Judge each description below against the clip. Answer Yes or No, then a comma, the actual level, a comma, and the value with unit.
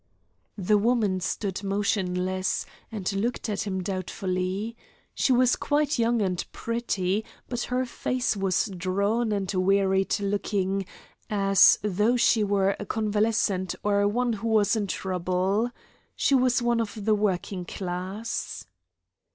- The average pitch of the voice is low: No, high, 205 Hz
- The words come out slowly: Yes, slow, 125 wpm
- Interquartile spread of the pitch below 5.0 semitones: Yes, average, 3.2 semitones